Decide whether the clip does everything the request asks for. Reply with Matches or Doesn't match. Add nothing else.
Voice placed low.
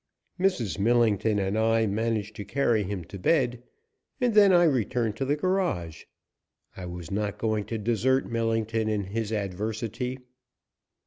Matches